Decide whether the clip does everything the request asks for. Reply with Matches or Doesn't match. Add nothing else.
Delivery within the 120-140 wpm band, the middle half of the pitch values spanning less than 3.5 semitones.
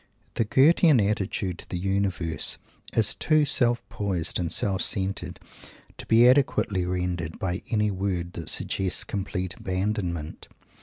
Matches